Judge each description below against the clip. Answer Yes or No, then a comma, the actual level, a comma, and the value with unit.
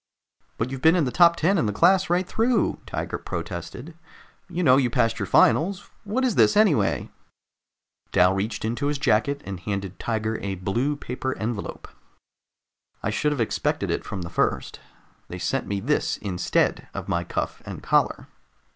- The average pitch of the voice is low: Yes, low, 125 Hz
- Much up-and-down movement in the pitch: Yes, wide, 8.5 semitones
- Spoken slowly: No, average, 175 wpm